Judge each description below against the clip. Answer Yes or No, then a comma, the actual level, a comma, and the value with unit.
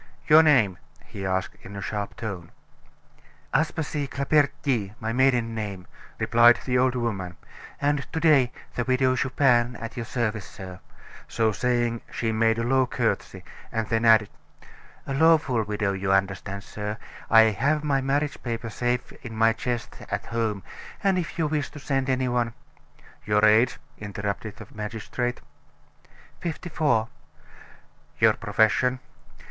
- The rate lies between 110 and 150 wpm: Yes, average, 145 wpm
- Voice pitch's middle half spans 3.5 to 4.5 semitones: Yes, average, 3.8 semitones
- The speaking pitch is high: No, low, 120 Hz